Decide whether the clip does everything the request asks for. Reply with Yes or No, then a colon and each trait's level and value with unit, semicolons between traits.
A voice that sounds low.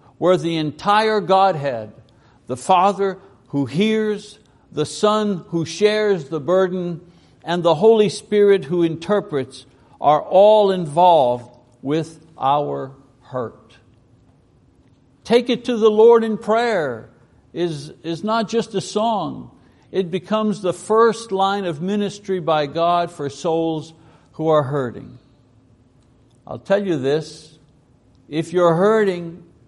No: medium, 170 Hz